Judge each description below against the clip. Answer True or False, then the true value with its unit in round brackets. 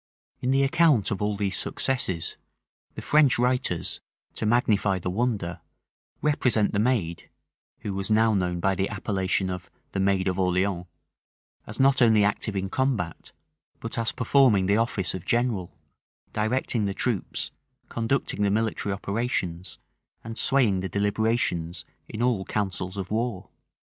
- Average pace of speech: True (145 wpm)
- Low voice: True (105 Hz)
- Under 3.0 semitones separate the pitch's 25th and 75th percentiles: False (3.9 semitones)